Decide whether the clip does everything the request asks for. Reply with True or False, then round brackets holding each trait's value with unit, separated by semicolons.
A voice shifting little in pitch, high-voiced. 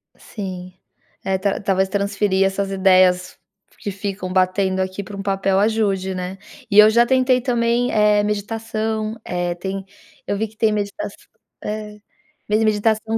True (2.2 semitones; 200 Hz)